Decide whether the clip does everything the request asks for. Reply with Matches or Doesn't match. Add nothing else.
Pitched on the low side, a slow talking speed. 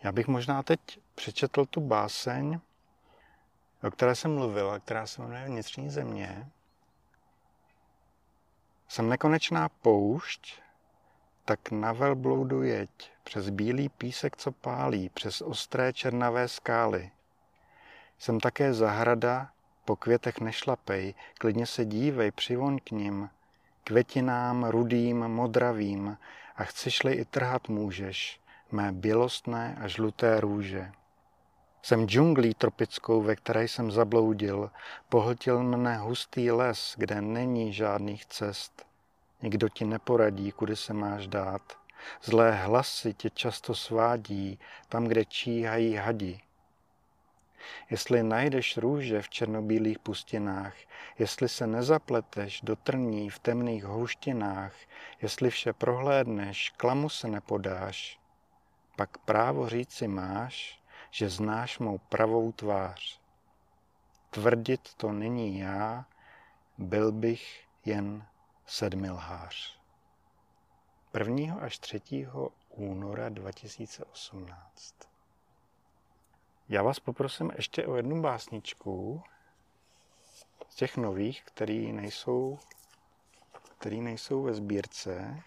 Matches